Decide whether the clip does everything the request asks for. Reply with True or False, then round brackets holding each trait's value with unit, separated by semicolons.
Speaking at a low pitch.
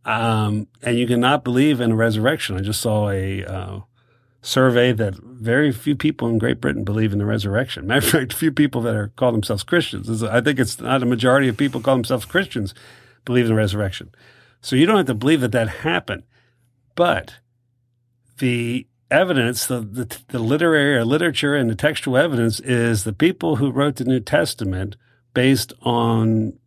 True (120 Hz)